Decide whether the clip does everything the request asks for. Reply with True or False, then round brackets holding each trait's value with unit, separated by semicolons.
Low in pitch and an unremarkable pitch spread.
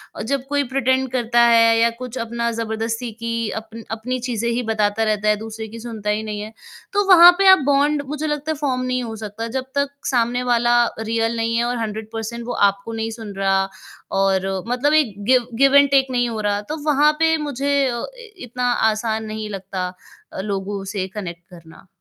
False (230 Hz; 3.1 semitones)